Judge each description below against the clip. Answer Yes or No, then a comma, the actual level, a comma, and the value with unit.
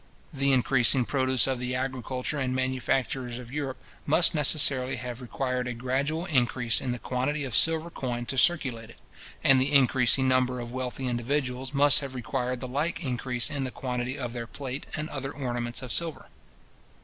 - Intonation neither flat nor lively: No, narrow, 1.9 semitones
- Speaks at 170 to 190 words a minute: Yes, average, 175 wpm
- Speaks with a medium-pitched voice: No, low, 130 Hz